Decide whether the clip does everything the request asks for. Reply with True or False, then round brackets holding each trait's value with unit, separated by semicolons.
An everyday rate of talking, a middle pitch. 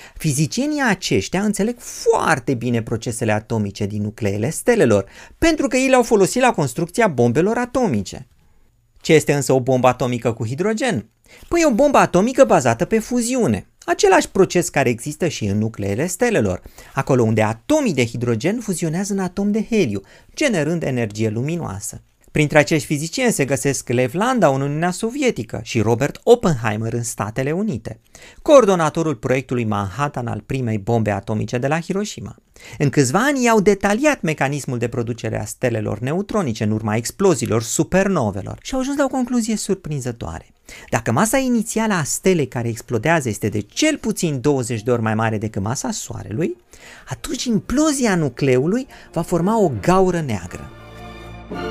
True (150 wpm; 150 Hz)